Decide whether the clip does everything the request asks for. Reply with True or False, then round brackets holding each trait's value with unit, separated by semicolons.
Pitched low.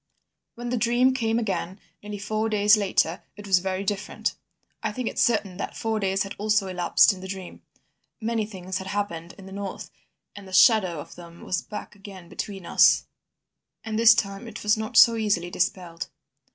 False (200 Hz)